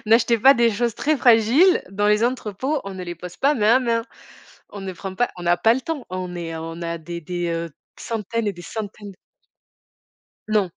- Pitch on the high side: Yes, high, 210 Hz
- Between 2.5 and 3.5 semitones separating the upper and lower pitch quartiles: No, average, 5.0 semitones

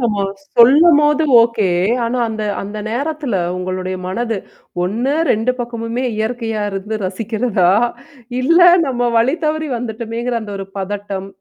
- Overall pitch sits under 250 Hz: Yes, high, 230 Hz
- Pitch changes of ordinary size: Yes, average, 3.4 semitones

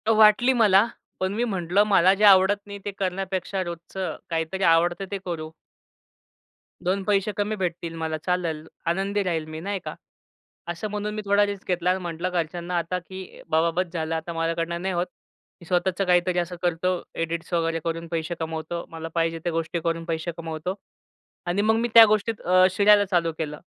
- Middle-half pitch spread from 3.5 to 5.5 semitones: No, average, 2.9 semitones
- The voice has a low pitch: No, medium, 180 Hz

